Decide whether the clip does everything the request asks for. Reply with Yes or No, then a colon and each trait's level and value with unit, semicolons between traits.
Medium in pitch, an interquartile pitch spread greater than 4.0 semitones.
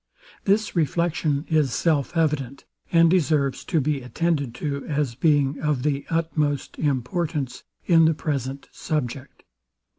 No: medium, 150 Hz; average, 2.9 semitones